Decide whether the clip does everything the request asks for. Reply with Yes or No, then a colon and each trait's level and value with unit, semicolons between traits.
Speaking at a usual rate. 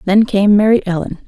Yes: average, 190 wpm